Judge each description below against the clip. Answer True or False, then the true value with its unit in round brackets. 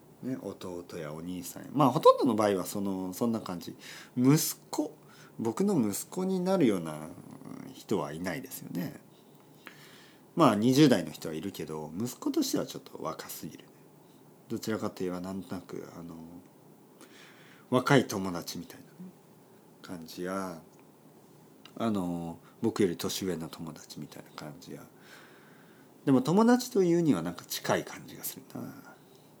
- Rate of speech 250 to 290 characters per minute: True (270 characters per minute)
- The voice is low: True (105 Hz)